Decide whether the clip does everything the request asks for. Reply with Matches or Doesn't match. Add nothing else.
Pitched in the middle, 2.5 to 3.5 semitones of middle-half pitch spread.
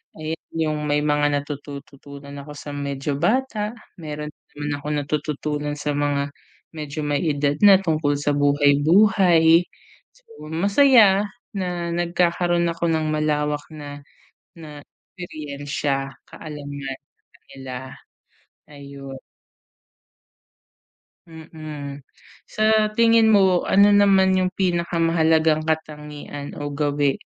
Matches